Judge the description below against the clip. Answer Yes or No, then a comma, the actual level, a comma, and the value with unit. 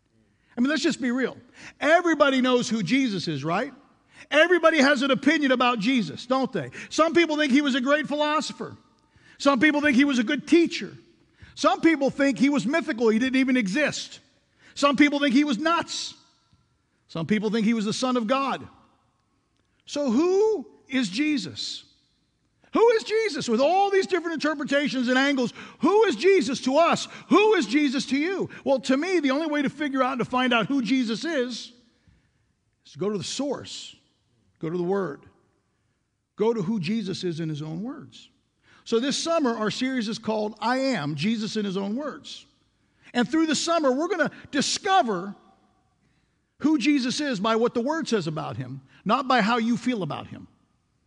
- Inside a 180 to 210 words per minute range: Yes, average, 185 wpm